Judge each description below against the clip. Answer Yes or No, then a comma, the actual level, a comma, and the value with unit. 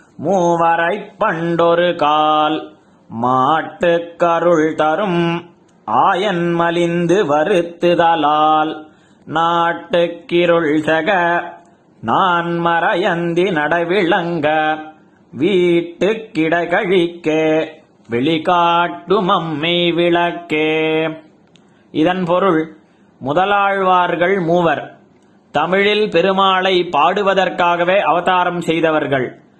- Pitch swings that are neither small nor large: No, narrow, 1.8 semitones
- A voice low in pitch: No, medium, 170 Hz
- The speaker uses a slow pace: Yes, slow, 50 wpm